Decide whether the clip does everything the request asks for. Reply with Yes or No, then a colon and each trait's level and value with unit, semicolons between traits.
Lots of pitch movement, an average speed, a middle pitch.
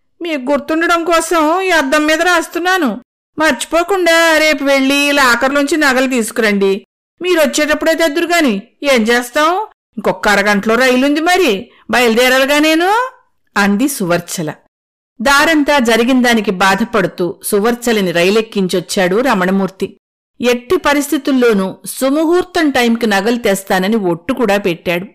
No: wide, 7.2 semitones; average, 95 wpm; very high, 265 Hz